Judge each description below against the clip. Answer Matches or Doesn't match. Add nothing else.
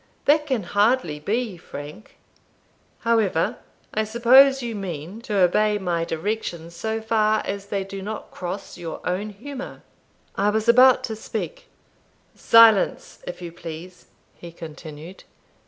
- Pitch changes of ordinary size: Matches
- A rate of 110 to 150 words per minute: Matches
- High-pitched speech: Matches